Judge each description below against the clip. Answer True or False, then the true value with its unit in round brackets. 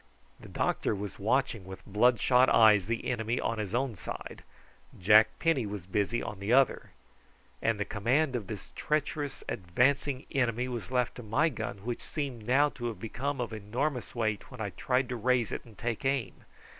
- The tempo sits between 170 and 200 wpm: True (180 wpm)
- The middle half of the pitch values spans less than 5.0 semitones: True (3.6 semitones)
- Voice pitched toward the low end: True (120 Hz)